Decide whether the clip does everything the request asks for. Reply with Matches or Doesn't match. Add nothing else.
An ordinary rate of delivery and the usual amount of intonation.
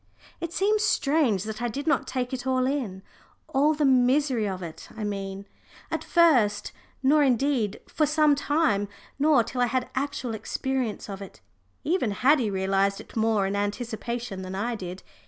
Doesn't match